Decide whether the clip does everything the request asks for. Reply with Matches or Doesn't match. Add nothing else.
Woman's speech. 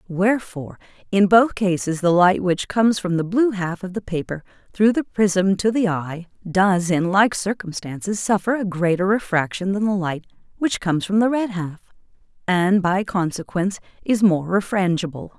Matches